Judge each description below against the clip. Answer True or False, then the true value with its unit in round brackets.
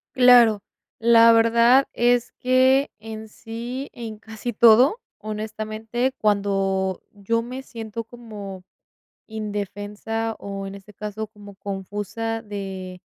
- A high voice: True (220 Hz)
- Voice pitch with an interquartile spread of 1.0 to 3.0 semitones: True (2.4 semitones)